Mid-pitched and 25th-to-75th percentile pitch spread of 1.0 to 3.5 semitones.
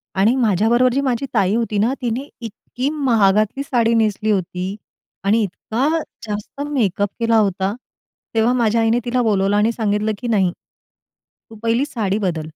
No: high, 225 Hz; average, 3.0 semitones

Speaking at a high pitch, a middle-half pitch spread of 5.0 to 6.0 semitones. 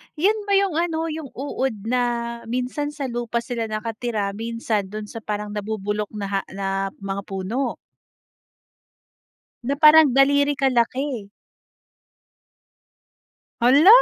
Yes: high, 240 Hz; wide, 5.4 semitones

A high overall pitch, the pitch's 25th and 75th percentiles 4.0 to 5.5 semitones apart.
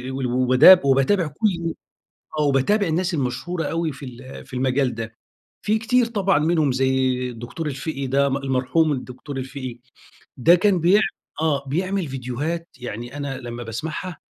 No: medium, 140 Hz; average, 4.7 semitones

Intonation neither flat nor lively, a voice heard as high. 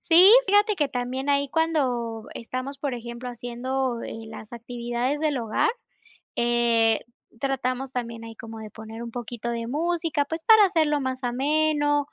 Yes: average, 3.7 semitones; very high, 255 Hz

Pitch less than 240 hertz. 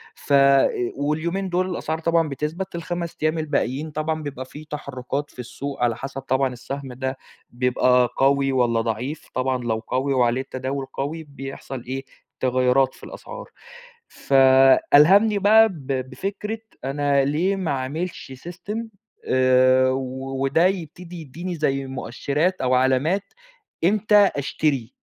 Yes: medium, 140 Hz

